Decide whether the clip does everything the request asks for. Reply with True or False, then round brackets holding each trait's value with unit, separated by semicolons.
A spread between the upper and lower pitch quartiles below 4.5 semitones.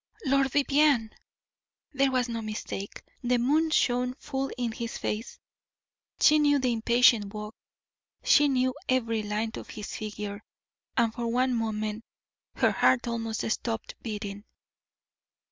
True (3.0 semitones)